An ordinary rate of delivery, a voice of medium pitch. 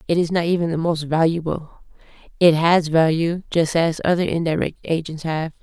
Yes: average, 170 wpm; medium, 165 Hz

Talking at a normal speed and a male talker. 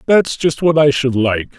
No: fast, 225 wpm; male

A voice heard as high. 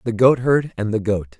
No: low, 115 Hz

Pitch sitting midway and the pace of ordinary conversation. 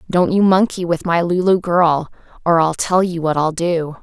No: medium, 170 Hz; fast, 210 wpm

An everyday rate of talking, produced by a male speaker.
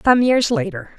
No: average, 185 wpm; female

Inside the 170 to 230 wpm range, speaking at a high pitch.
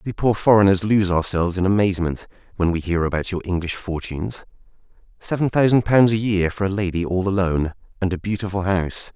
No: average, 185 wpm; very low, 95 Hz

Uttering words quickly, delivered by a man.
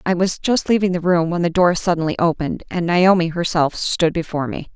No: fast, 215 wpm; female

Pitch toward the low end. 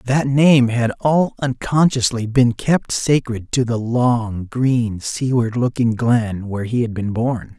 Yes: low, 120 Hz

